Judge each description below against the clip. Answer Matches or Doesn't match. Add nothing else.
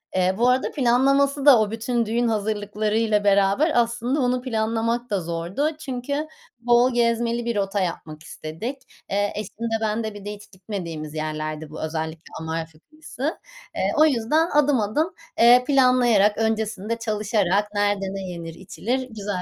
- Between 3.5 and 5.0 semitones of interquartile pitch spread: Matches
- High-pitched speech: Matches